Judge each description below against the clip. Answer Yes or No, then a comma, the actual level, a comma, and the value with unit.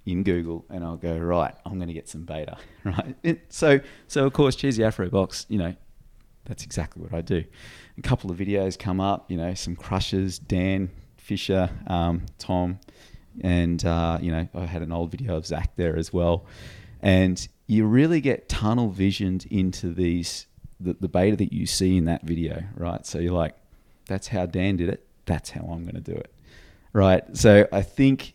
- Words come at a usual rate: Yes, average, 195 wpm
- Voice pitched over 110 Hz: No, very low, 95 Hz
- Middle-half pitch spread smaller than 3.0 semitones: No, average, 3.3 semitones